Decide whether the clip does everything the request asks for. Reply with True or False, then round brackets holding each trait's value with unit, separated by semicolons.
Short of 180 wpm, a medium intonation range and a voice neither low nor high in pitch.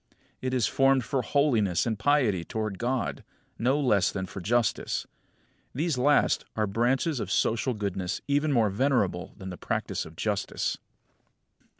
False (150 wpm; 5.0 semitones; 115 Hz)